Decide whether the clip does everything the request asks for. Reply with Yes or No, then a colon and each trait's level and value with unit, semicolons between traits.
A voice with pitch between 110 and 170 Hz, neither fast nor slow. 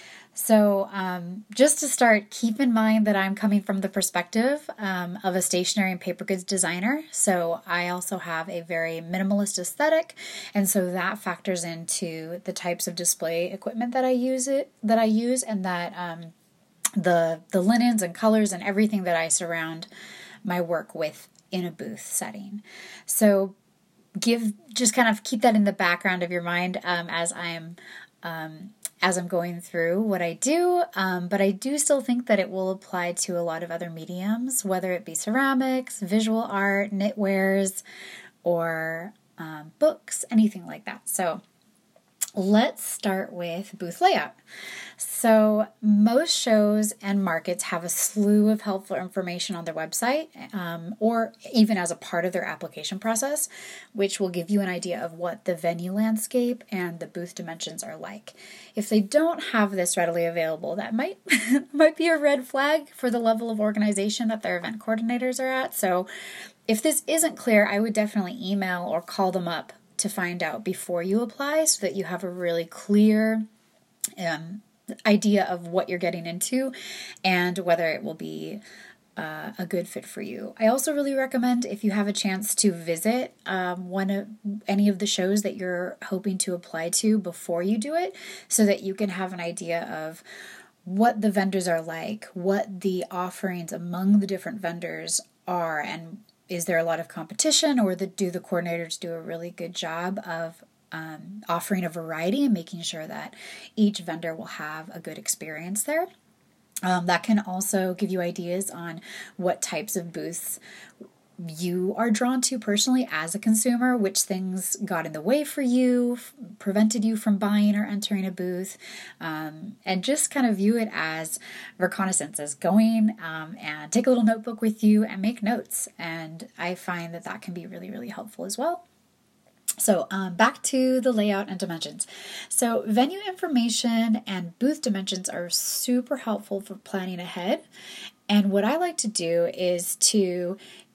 No: high, 195 Hz; average, 180 wpm